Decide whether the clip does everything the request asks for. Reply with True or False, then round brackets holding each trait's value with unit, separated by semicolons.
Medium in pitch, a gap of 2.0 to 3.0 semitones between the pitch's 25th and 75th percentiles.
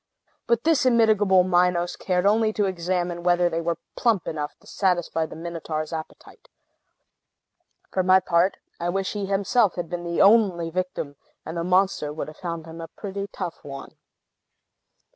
True (180 Hz; 2.7 semitones)